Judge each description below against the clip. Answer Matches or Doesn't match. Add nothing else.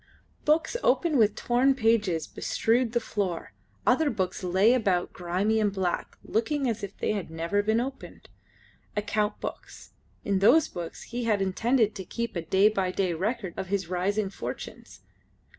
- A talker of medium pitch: Doesn't match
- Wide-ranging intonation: Doesn't match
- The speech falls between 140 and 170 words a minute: Matches